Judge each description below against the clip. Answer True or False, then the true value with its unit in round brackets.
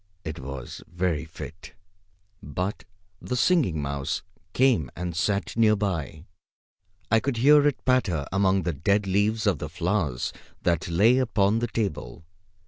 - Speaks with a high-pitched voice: False (95 Hz)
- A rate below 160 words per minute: True (140 wpm)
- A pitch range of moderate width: False (5.9 semitones)